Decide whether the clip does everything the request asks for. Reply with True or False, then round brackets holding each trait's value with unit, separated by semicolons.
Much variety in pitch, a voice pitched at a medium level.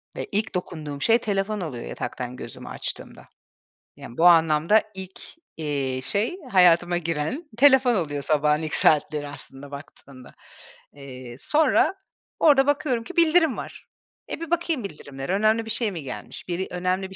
True (7.7 semitones; 180 Hz)